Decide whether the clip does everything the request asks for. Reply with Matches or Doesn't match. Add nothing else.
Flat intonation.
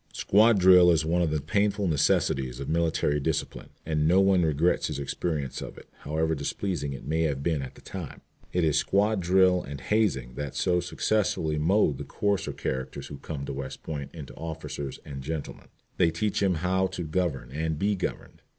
Doesn't match